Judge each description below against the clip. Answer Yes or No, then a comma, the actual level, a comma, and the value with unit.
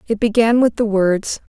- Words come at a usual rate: Yes, average, 195 wpm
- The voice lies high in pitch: Yes, high, 215 Hz